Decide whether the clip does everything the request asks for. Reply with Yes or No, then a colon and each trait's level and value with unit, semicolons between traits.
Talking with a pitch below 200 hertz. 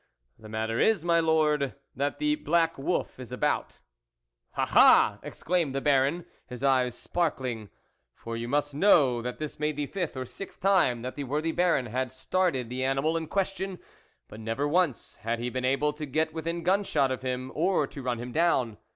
Yes: medium, 140 Hz